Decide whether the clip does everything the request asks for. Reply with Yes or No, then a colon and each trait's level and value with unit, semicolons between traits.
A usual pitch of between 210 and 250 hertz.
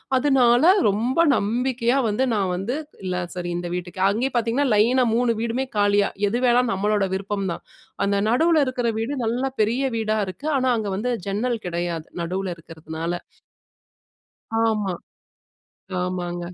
Yes: high, 215 Hz